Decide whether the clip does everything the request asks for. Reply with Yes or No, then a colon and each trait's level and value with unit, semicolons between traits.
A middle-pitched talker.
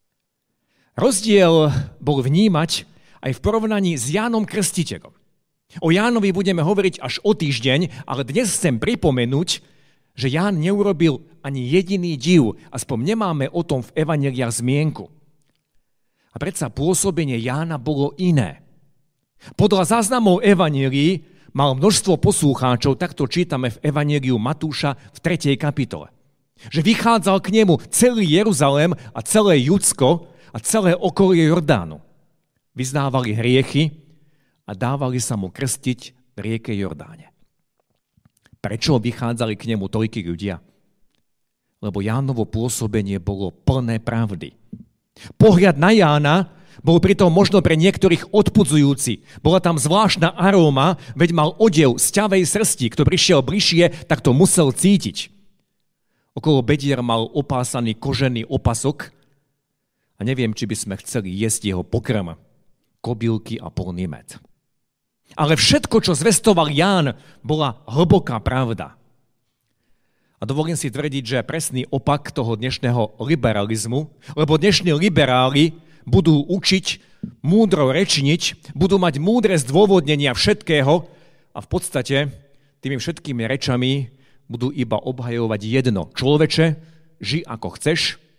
Yes: medium, 145 Hz